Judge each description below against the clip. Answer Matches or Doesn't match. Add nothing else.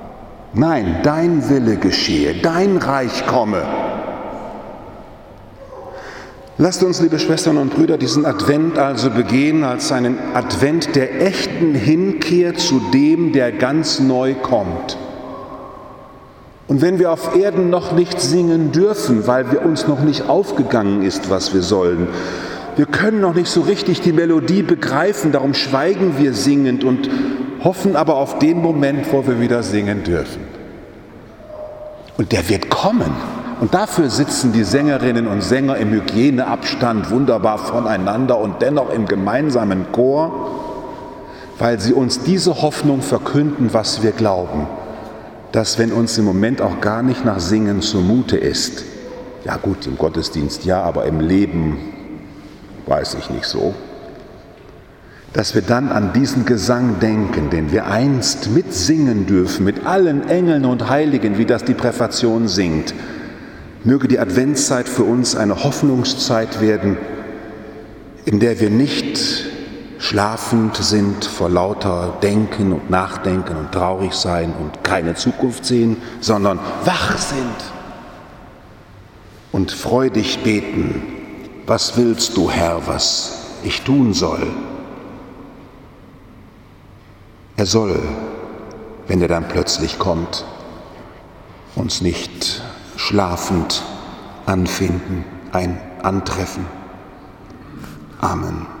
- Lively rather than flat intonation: Matches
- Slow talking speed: Matches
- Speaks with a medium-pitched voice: Doesn't match